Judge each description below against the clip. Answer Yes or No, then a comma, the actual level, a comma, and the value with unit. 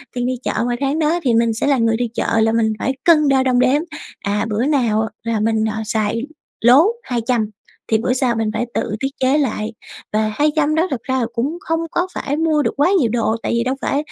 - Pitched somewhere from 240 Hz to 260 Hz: Yes, high, 245 Hz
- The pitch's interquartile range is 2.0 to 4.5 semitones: Yes, average, 4.2 semitones